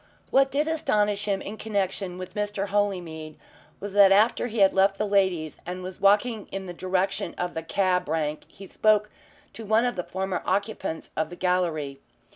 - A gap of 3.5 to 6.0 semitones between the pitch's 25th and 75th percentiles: No, narrow, 2.5 semitones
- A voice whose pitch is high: Yes, high, 195 Hz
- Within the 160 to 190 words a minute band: Yes, average, 185 wpm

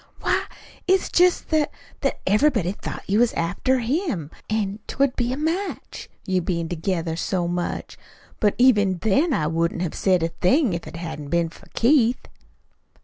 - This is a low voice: No, high, 200 Hz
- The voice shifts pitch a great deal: Yes, wide, 7.3 semitones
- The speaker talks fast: No, average, 165 wpm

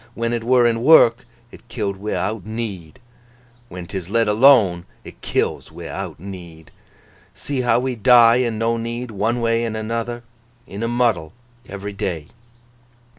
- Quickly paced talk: No, average, 140 wpm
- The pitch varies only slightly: No, average, 3.1 semitones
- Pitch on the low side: Yes, low, 115 Hz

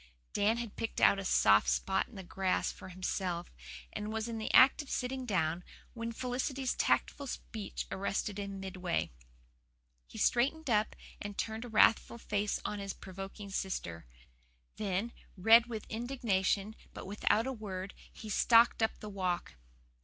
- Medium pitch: No, high, 210 Hz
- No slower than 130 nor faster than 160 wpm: Yes, average, 155 wpm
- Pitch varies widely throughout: No, average, 3.3 semitones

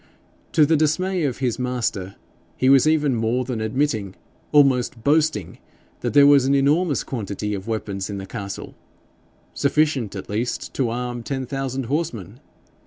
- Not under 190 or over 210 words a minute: No, average, 155 wpm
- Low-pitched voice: Yes, low, 125 Hz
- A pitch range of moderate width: Yes, average, 4.6 semitones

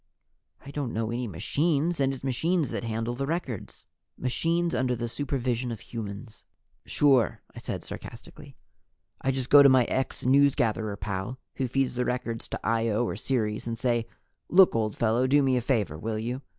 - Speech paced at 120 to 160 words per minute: No, average, 175 wpm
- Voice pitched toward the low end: Yes, low, 125 Hz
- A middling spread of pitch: Yes, average, 3.2 semitones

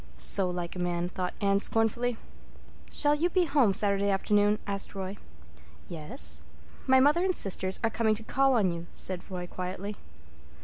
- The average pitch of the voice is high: Yes, high, 200 Hz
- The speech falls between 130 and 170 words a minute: Yes, average, 165 wpm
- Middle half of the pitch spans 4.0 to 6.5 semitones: Yes, average, 4.4 semitones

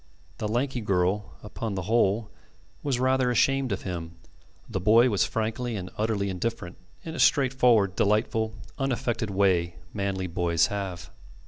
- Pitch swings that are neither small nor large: Yes, average, 4.2 semitones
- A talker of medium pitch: No, low, 105 Hz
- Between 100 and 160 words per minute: Yes, average, 140 wpm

